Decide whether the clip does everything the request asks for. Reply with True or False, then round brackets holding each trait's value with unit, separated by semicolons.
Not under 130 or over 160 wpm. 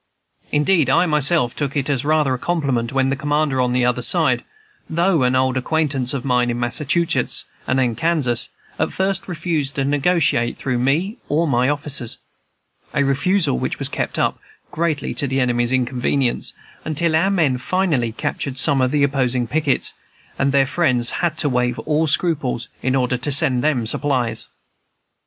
False (170 wpm)